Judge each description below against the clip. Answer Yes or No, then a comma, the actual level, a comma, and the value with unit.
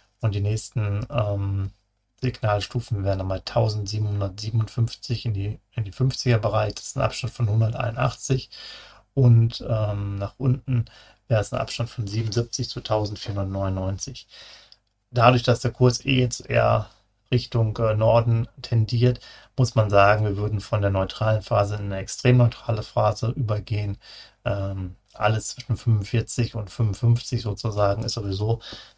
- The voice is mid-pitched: No, low, 110 Hz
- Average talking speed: Yes, average, 135 wpm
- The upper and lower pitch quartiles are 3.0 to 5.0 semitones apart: No, narrow, 2.6 semitones